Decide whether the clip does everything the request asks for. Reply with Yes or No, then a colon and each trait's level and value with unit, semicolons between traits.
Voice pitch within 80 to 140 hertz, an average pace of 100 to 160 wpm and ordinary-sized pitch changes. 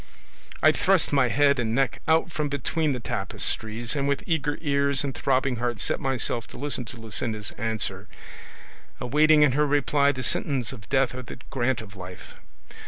No: low, 135 Hz; average, 175 wpm; average, 3.5 semitones